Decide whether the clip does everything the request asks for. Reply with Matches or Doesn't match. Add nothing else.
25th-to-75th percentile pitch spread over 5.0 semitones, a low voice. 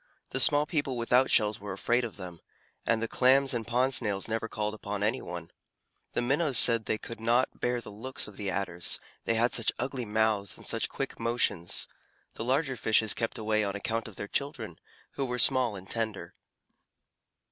Doesn't match